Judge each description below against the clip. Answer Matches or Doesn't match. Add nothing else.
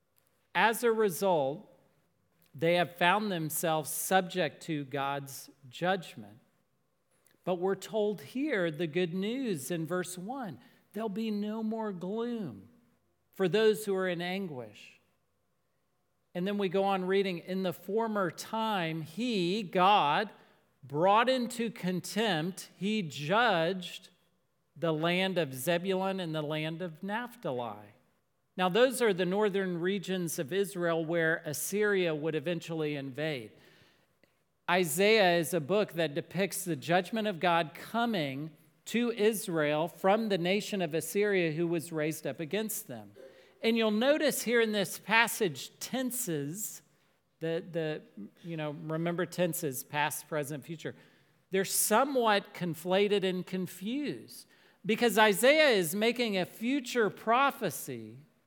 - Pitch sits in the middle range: Matches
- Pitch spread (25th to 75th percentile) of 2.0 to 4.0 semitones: Doesn't match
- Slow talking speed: Matches